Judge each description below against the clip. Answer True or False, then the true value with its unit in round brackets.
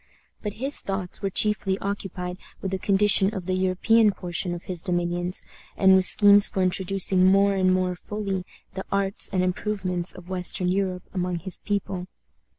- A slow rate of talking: False (165 wpm)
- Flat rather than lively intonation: True (1.6 semitones)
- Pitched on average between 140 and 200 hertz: True (190 Hz)